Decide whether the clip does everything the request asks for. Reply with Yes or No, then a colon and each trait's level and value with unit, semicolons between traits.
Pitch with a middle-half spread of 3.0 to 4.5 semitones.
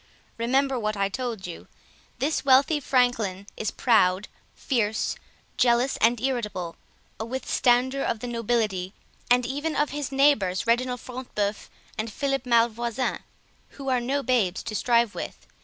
Yes: average, 3.5 semitones